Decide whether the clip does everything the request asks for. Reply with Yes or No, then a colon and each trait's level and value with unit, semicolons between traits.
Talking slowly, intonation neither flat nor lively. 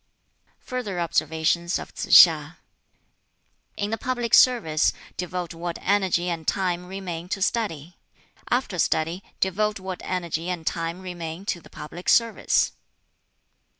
Yes: slow, 125 wpm; average, 3.1 semitones